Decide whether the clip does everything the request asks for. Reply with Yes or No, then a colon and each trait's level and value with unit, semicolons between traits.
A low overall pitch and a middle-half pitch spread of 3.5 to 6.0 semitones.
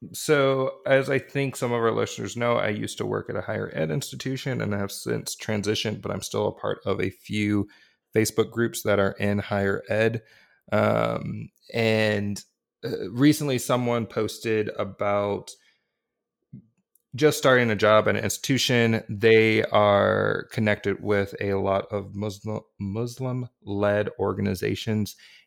No: low, 110 Hz; average, 2.9 semitones